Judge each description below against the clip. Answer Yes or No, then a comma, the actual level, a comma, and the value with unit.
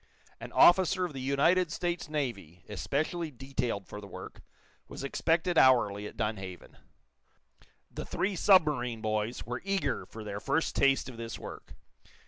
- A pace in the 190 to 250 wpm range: No, average, 145 wpm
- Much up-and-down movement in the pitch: Yes, wide, 7.2 semitones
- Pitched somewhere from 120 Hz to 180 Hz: Yes, low, 135 Hz